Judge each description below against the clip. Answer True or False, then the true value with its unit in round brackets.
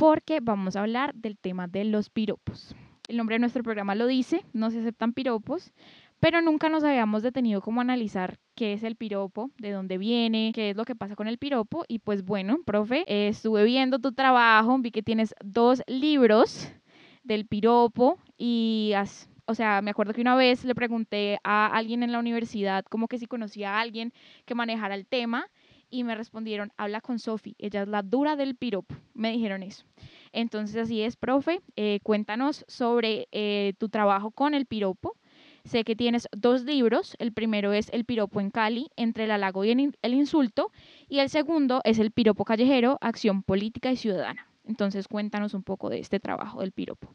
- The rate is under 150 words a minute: False (190 wpm)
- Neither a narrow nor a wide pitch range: True (3.2 semitones)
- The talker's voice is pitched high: True (225 Hz)